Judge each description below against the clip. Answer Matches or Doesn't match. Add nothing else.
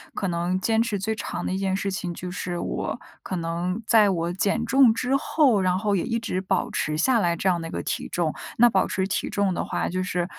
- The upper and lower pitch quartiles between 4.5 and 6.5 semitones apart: Doesn't match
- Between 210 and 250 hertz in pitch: Doesn't match